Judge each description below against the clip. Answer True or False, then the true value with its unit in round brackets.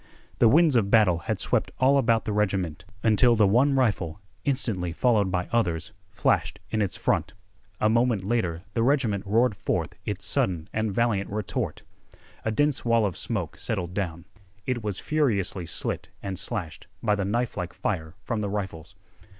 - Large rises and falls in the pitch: False (4.1 semitones)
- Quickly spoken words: False (165 wpm)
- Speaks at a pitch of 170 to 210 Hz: False (105 Hz)